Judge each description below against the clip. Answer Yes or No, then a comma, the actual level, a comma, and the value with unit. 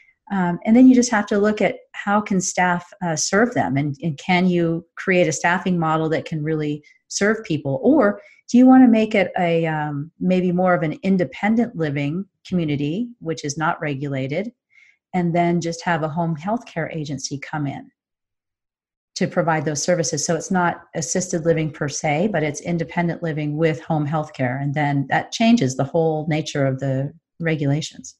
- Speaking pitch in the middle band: Yes, medium, 165 Hz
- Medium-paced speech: Yes, average, 185 wpm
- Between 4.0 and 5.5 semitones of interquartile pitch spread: No, average, 3.4 semitones